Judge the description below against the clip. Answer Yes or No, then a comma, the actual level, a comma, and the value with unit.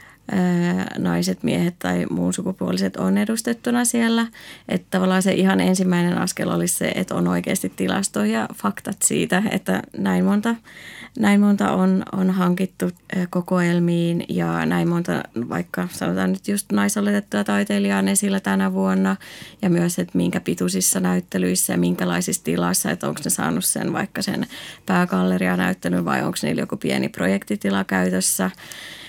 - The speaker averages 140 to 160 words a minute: Yes, average, 145 wpm